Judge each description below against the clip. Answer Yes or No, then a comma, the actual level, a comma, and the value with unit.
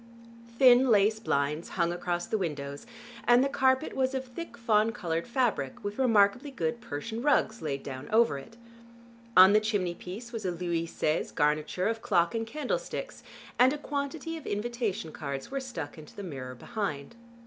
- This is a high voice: Yes, high, 215 Hz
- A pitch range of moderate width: No, wide, 6.7 semitones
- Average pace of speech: Yes, average, 170 wpm